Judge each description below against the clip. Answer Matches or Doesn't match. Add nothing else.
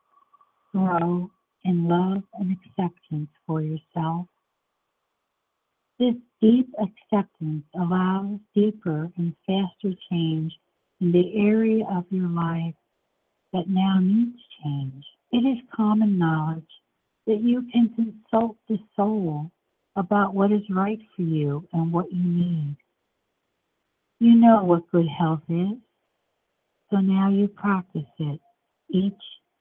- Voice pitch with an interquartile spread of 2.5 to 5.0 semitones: Matches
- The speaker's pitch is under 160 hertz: Doesn't match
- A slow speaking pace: Matches